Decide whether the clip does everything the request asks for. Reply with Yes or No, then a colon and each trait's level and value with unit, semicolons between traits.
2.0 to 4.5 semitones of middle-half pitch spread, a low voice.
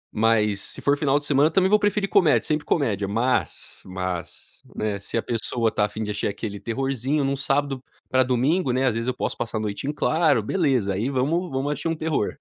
No: average, 5.2 semitones; low, 130 Hz